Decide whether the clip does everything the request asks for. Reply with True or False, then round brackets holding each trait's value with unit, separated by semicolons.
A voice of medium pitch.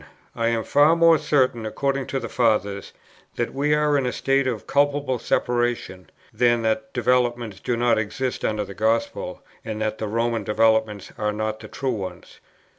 False (115 Hz)